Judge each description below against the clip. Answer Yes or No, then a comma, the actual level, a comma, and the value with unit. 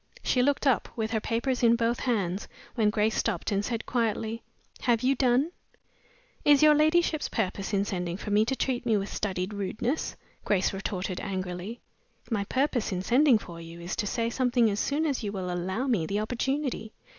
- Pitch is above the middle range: Yes, high, 225 Hz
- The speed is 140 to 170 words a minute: No, average, 190 wpm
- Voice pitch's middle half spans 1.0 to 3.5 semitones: No, average, 4.4 semitones